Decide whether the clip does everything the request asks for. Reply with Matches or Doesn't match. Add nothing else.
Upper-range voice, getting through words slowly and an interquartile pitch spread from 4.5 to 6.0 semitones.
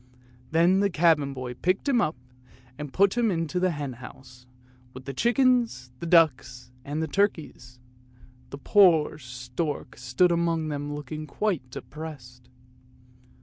Doesn't match